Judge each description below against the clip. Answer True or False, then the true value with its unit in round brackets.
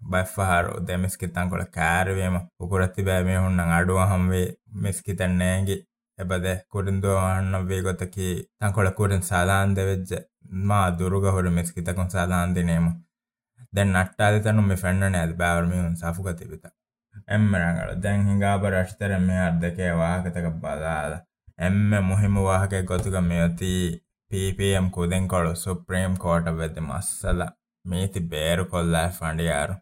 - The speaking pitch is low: True (90 Hz)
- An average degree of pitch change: False (1.7 semitones)